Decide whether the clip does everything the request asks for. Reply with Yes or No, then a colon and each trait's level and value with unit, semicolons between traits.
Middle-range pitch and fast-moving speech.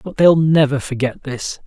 No: medium, 145 Hz; average, 180 wpm